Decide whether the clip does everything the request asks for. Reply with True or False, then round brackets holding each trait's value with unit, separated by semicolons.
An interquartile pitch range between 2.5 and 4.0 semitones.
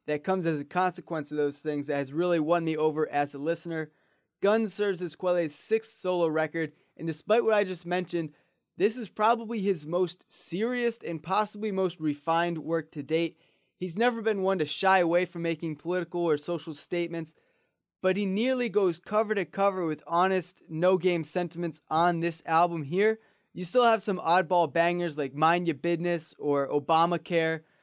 True (2.9 semitones)